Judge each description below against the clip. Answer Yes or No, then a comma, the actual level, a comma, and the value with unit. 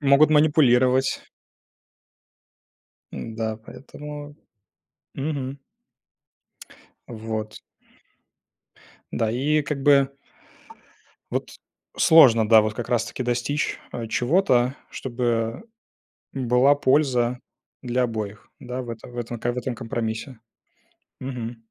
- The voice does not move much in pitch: No, average, 3.2 semitones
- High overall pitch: No, low, 125 Hz